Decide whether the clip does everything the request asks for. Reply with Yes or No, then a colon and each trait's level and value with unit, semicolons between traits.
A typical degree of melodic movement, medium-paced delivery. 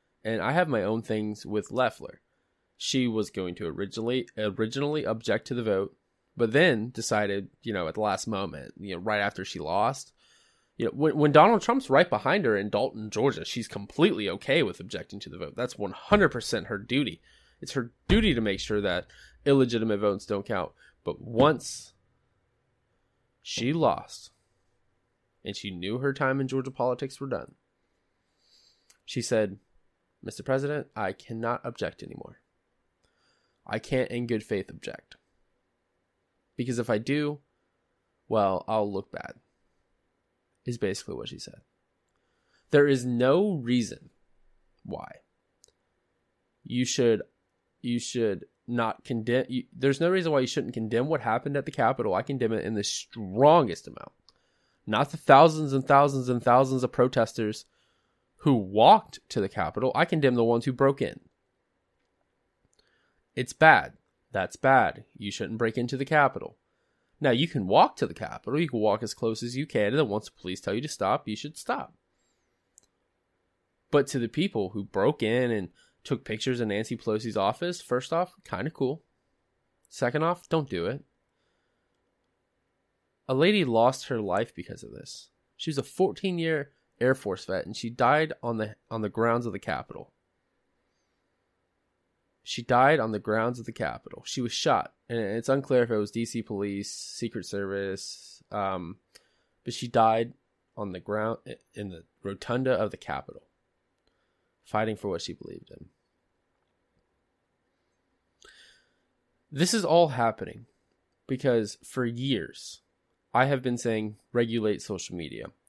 Yes: average, 4.2 semitones; average, 160 wpm